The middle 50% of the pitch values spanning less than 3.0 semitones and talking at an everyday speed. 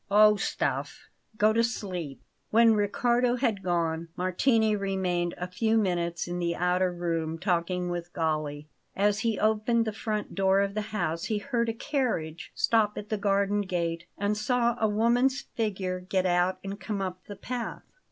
No: average, 3.7 semitones; average, 170 wpm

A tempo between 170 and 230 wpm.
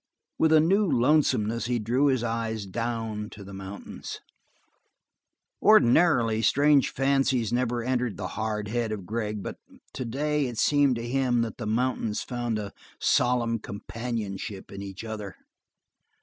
No: average, 140 wpm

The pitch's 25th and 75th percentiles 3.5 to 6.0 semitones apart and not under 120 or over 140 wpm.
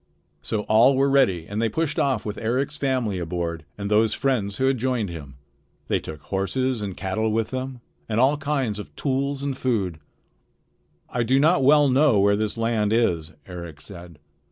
No: average, 5.1 semitones; average, 180 wpm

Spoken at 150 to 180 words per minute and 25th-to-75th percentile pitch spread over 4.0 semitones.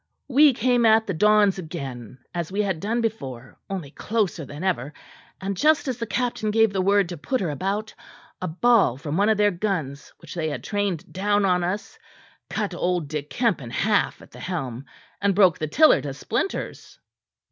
No: average, 190 wpm; wide, 5.5 semitones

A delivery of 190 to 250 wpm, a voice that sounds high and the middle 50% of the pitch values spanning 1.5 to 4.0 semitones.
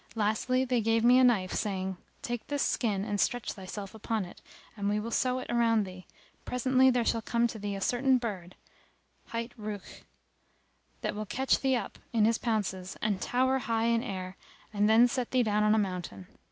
Yes: average, 195 wpm; high, 225 Hz; average, 3.3 semitones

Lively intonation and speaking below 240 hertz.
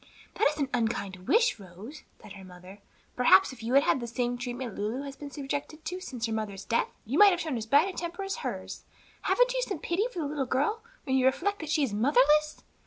No: wide, 5.8 semitones; very high, 270 Hz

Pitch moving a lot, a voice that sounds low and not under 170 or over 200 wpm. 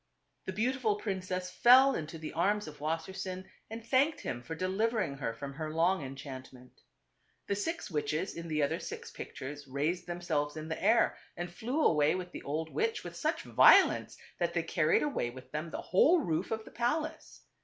No: wide, 6.4 semitones; medium, 175 Hz; average, 185 wpm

